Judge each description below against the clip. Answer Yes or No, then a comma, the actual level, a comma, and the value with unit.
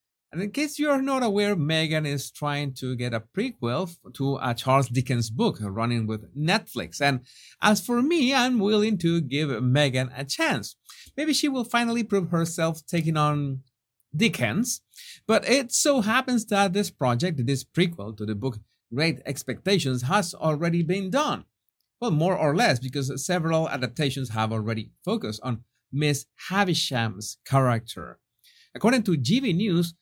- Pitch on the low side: No, medium, 155 Hz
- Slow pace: No, average, 155 wpm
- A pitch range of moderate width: No, wide, 7.9 semitones